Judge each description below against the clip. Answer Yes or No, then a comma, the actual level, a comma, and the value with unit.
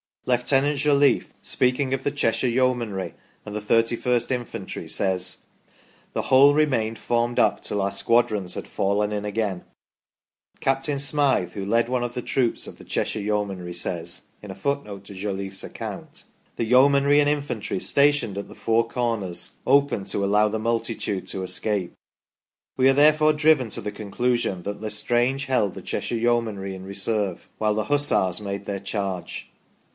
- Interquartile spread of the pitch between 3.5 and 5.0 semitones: Yes, average, 4.6 semitones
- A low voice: Yes, low, 115 Hz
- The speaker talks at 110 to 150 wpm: No, average, 165 wpm